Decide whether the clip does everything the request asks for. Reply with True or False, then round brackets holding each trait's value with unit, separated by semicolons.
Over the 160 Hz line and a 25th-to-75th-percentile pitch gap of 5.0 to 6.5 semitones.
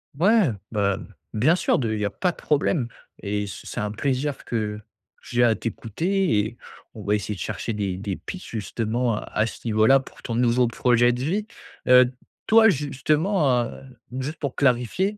False (120 Hz; 5.5 semitones)